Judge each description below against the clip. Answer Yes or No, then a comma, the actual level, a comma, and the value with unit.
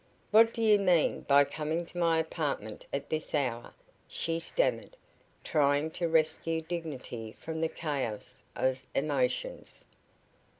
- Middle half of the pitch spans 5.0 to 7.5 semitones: No, average, 3.1 semitones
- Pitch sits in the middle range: Yes, medium, 155 Hz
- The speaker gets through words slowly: Yes, slow, 130 wpm